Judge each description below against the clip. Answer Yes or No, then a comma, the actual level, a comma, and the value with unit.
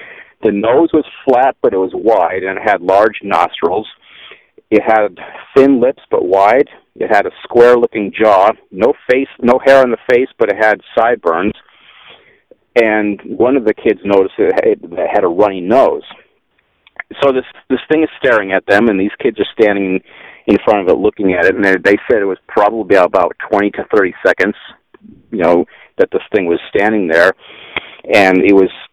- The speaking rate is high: No, average, 185 wpm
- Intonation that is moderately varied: No, wide, 7.3 semitones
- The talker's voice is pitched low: Yes, low, 125 Hz